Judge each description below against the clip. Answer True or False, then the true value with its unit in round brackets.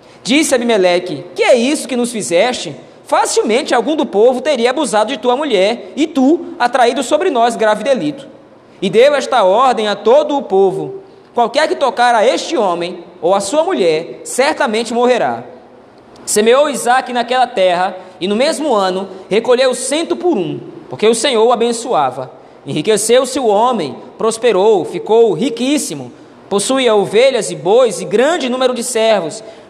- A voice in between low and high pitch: False (250 Hz)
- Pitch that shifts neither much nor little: False (5.8 semitones)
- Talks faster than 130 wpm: True (155 wpm)